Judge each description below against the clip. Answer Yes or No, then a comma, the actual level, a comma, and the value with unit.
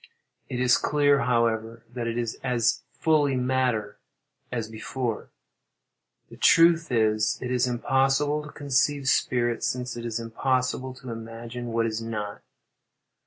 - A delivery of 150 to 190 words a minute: No, slow, 135 wpm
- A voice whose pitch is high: No, low, 125 Hz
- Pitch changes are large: No, narrow, 2.5 semitones